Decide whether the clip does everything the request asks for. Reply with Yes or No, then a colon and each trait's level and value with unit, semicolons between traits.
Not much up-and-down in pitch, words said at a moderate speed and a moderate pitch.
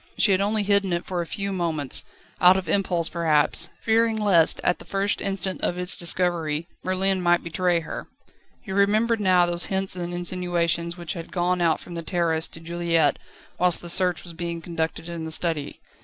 Yes: narrow, 2.2 semitones; average, 190 wpm; medium, 175 Hz